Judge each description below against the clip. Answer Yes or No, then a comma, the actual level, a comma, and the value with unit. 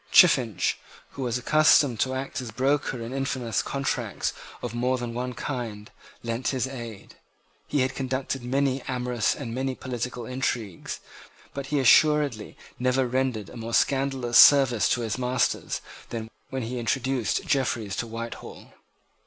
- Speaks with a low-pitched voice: Yes, low, 125 Hz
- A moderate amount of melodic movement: No, narrow, 2.3 semitones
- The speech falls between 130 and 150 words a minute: Yes, average, 145 wpm